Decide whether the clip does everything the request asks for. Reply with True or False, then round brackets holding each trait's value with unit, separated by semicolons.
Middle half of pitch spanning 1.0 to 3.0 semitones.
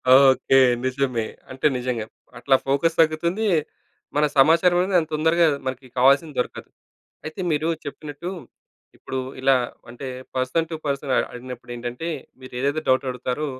False (3.7 semitones)